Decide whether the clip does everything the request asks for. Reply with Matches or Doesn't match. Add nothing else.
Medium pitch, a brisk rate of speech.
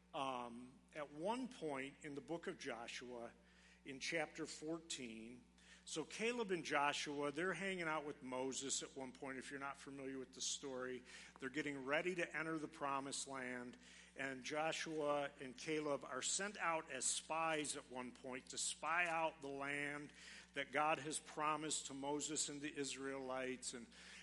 Doesn't match